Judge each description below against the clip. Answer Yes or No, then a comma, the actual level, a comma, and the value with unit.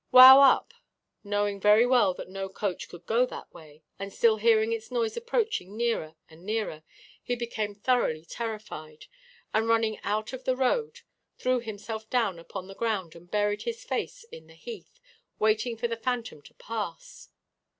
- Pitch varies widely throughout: No, average, 3.7 semitones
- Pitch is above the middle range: Yes, high, 220 Hz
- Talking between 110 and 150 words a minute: No, average, 170 wpm